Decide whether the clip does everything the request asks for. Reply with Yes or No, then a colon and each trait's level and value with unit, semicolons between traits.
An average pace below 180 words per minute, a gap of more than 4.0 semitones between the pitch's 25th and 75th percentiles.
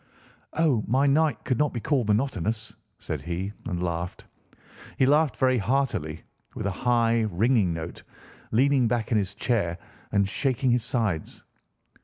Yes: average, 150 wpm; average, 5.3 semitones